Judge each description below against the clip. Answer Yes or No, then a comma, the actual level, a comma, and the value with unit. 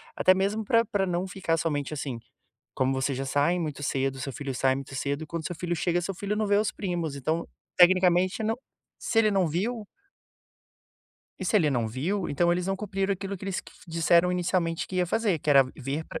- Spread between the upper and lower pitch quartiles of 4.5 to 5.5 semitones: Yes, average, 5.0 semitones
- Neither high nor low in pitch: Yes, medium, 175 Hz